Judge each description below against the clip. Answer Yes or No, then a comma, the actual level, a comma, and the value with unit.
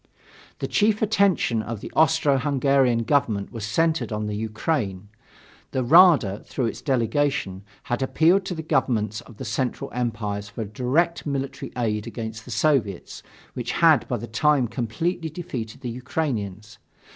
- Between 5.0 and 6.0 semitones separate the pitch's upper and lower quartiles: Yes, wide, 5.6 semitones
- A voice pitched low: Yes, low, 125 Hz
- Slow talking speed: No, average, 150 wpm